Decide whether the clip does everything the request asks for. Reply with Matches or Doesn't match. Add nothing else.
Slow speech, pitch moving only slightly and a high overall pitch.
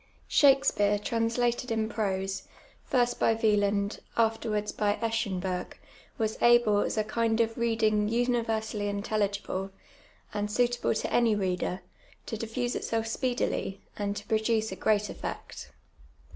Matches